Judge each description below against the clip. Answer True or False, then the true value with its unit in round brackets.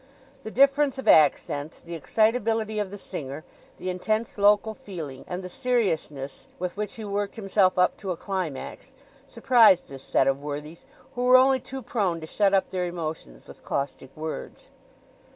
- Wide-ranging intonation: True (5.7 semitones)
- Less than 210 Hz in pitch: True (190 Hz)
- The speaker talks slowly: False (170 wpm)